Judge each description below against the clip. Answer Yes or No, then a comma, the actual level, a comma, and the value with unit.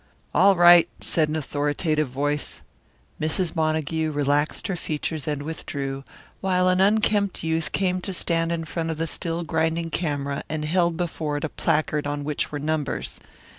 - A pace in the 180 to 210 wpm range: No, average, 165 wpm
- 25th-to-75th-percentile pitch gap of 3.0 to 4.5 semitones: No, narrow, 2.6 semitones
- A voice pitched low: No, medium, 160 Hz